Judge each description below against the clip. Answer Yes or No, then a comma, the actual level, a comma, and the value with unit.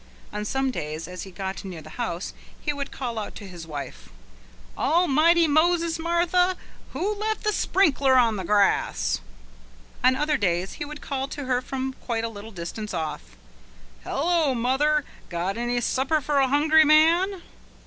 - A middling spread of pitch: No, wide, 7.6 semitones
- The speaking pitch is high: Yes, very high, 265 Hz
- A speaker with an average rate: Yes, average, 165 wpm